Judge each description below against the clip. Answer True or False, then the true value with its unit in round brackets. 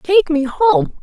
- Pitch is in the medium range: False (320 Hz)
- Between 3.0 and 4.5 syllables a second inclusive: True (4.3 syllables/s)